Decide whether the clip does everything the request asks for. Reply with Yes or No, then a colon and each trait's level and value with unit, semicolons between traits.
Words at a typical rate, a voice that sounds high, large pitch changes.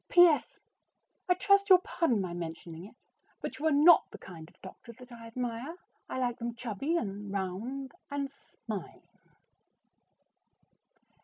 Yes: average, 150 wpm; high, 240 Hz; wide, 6.5 semitones